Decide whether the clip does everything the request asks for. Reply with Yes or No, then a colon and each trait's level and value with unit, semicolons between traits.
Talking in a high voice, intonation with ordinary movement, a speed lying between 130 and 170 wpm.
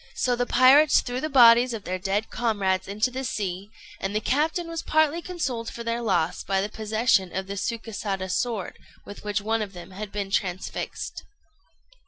No: high, 215 Hz; average, 4.2 semitones; average, 185 wpm